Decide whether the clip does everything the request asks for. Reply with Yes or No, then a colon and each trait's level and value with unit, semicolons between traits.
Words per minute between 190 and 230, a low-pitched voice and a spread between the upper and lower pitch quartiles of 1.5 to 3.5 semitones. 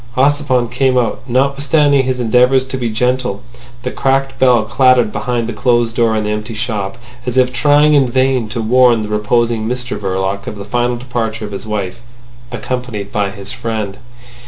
No: average, 175 wpm; low, 120 Hz; average, 2.9 semitones